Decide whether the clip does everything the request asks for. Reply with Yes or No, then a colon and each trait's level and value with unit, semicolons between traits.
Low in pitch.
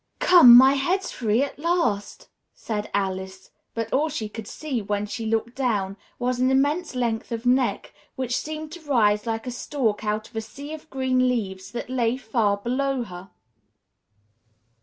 No: high, 240 Hz